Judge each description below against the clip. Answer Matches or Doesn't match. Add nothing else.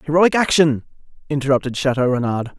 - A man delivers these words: Matches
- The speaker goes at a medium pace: Doesn't match